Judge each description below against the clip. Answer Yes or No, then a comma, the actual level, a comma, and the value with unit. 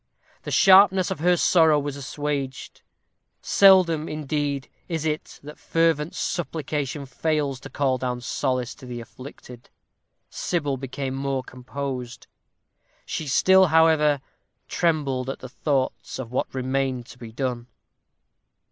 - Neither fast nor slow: No, slow, 125 wpm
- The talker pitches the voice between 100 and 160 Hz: Yes, medium, 140 Hz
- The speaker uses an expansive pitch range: No, average, 3.4 semitones